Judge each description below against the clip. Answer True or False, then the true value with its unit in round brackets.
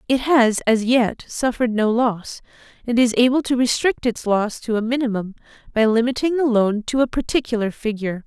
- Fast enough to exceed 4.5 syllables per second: True (5.3 syllables/s)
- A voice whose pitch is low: False (235 Hz)